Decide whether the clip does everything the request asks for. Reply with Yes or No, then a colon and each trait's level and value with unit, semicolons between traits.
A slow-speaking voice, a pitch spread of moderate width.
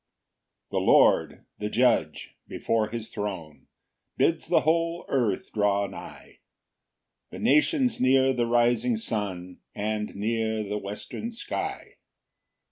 Yes: slow, 120 wpm; average, 3.8 semitones